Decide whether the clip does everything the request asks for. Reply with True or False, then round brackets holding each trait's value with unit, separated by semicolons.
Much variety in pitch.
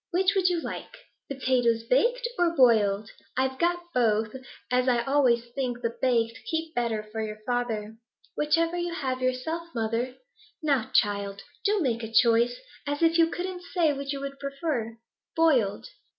True (6.1 semitones)